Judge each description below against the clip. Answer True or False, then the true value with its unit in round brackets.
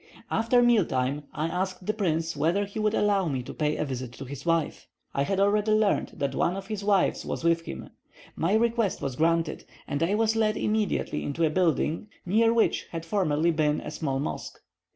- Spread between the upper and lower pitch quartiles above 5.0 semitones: True (5.5 semitones)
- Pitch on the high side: False (175 Hz)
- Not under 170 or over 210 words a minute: True (205 wpm)